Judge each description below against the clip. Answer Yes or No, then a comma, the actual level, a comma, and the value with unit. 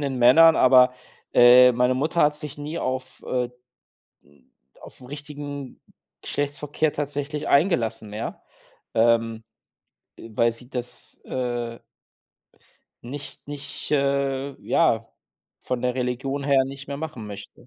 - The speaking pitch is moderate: No, low, 130 Hz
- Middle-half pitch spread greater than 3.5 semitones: No, average, 2.9 semitones